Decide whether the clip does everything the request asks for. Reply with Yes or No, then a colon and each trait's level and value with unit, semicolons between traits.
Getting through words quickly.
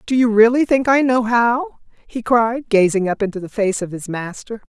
Yes: fast, 215 wpm